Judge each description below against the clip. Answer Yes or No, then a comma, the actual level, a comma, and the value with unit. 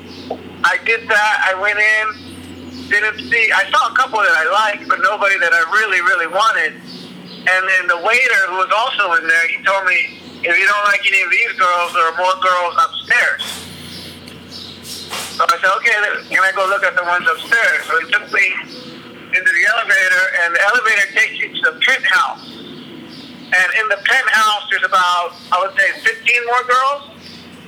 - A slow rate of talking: No, average, 185 wpm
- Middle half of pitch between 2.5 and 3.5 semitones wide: No, average, 5.3 semitones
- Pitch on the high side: Yes, high, 205 Hz